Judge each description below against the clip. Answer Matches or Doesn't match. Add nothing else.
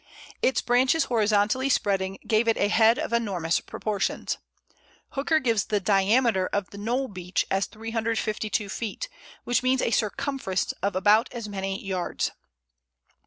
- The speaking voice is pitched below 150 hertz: Doesn't match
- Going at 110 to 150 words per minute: Matches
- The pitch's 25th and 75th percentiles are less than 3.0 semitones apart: Doesn't match